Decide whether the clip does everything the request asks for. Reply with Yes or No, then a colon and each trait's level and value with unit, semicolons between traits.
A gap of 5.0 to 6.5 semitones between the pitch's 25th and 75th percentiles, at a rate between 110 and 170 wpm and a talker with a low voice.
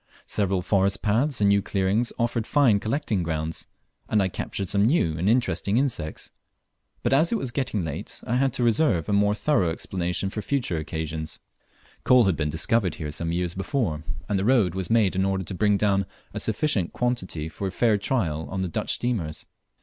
No: average, 5.3 semitones; average, 195 wpm; low, 100 Hz